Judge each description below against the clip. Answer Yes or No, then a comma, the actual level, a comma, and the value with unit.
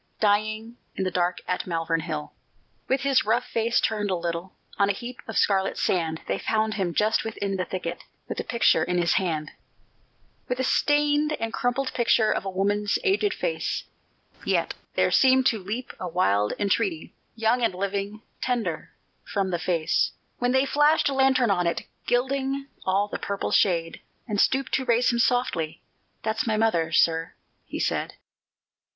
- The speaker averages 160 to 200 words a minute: Yes, average, 170 wpm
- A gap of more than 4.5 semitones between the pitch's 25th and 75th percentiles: Yes, average, 5.3 semitones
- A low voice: No, high, 210 Hz